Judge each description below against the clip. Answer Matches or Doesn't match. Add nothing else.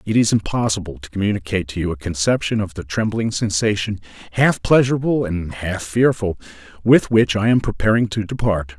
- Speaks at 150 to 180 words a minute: Matches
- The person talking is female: Doesn't match